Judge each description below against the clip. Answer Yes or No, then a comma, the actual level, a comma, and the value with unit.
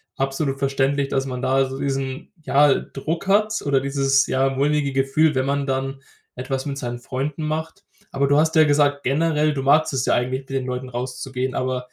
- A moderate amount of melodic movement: No, narrow, 1.6 semitones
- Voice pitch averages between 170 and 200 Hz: No, low, 135 Hz